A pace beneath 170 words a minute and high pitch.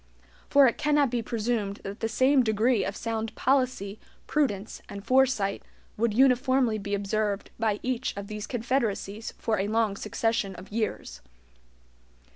Yes: average, 145 wpm; high, 225 Hz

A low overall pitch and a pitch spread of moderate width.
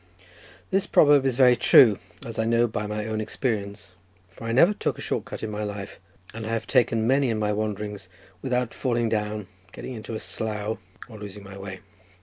No: low, 110 Hz; narrow, 2.3 semitones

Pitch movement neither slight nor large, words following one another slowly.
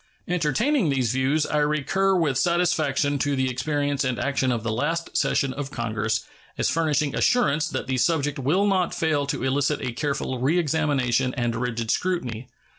No: average, 3.7 semitones; average, 165 wpm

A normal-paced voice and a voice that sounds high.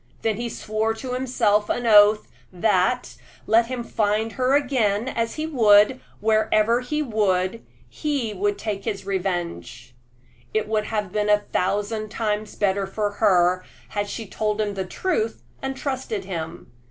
Yes: average, 155 wpm; high, 215 Hz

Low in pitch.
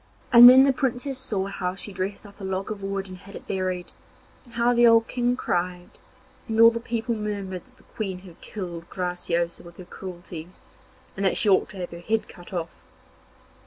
No: high, 195 Hz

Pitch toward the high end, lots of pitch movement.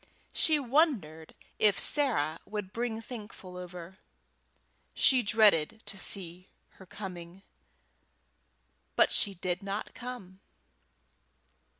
No: high, 195 Hz; average, 4.1 semitones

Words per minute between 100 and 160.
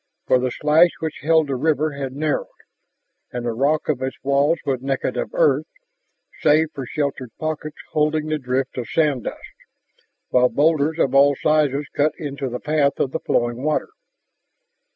No: average, 170 wpm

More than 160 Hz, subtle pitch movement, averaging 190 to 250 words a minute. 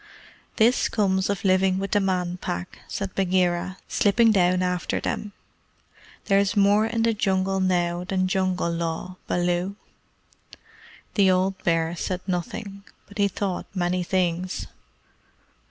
No: medium, 185 Hz; narrow, 1.9 semitones; slow, 135 wpm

